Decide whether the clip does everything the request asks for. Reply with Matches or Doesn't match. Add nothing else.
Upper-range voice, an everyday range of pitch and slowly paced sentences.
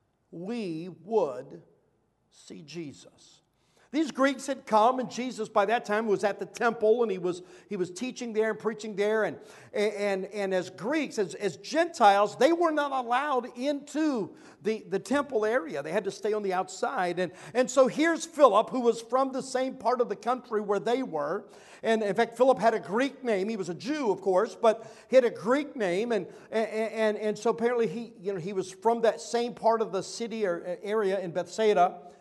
Doesn't match